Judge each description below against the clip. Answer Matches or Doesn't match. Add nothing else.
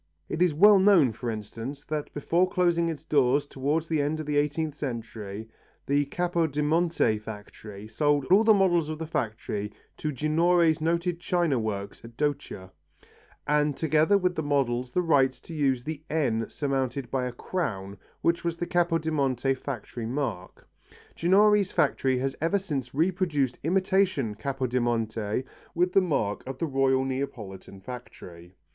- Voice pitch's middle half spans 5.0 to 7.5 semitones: Matches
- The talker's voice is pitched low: Doesn't match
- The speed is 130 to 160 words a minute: Matches